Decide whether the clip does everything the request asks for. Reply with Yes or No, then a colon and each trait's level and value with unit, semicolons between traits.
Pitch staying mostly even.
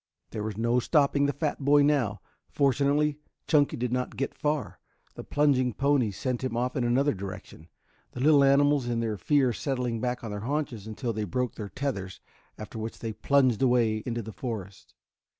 No: average, 4.1 semitones